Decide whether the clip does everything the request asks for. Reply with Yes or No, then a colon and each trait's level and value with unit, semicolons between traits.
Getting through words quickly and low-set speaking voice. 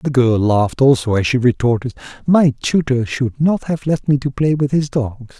Yes: fast, 210 wpm; low, 130 Hz